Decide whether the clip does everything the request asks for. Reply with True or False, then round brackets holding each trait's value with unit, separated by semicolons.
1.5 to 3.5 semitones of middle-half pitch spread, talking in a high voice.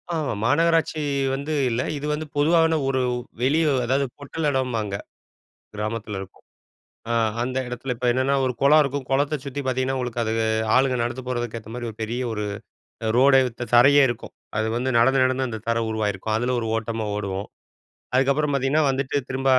False (3.2 semitones; 130 Hz)